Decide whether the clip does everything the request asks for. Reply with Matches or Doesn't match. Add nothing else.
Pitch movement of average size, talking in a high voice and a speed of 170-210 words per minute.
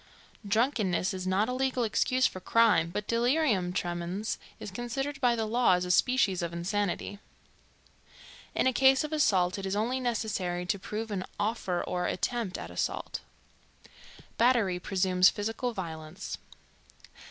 Doesn't match